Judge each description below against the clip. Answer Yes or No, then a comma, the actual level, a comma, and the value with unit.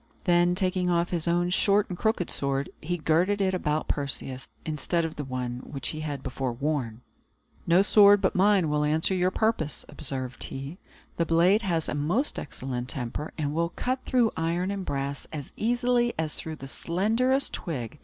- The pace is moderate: Yes, average, 180 wpm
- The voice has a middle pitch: Yes, medium, 165 Hz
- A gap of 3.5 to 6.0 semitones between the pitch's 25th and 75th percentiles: Yes, average, 5.0 semitones